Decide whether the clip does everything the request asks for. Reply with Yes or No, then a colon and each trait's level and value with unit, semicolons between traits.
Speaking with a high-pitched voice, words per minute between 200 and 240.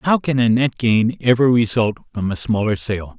No: low, 115 Hz; fast, 205 wpm